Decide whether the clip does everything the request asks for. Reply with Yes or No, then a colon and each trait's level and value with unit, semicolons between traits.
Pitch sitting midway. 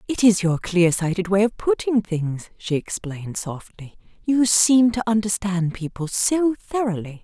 No: high, 200 Hz